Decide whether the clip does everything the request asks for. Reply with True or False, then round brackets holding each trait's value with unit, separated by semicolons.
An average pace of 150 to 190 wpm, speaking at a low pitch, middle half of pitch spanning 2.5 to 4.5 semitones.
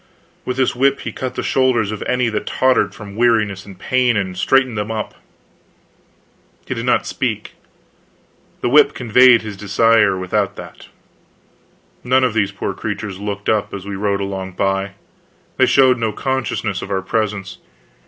True (165 wpm; 105 Hz; 4.0 semitones)